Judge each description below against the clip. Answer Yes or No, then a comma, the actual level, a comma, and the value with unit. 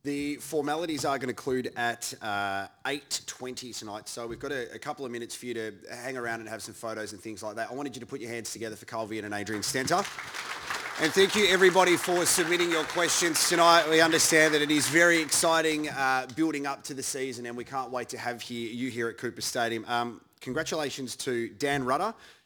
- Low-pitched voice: Yes, low, 130 Hz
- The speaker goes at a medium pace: No, fast, 225 wpm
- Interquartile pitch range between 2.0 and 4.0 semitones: No, average, 5.2 semitones